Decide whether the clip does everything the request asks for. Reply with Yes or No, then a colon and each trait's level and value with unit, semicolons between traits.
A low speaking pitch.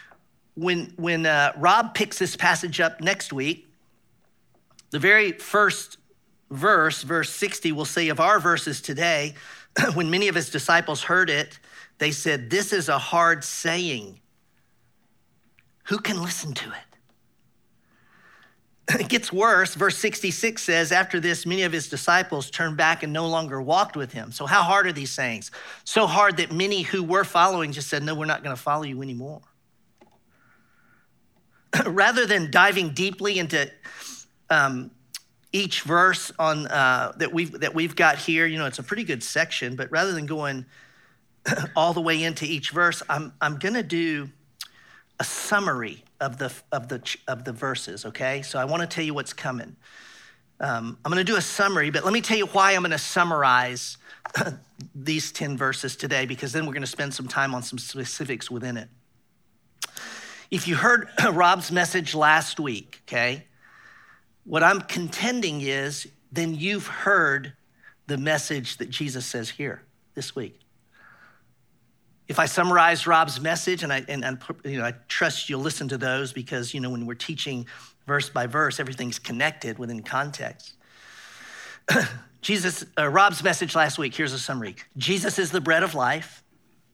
No: medium, 155 Hz